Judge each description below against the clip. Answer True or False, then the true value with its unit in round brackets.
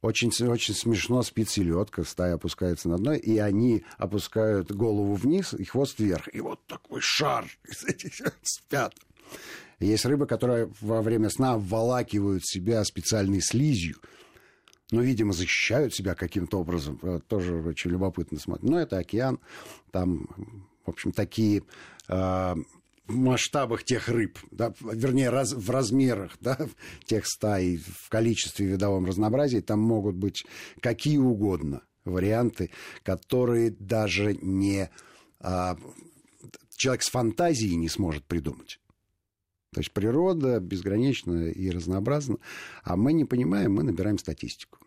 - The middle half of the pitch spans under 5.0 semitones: True (4.0 semitones)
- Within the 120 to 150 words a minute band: True (130 wpm)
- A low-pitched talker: True (105 Hz)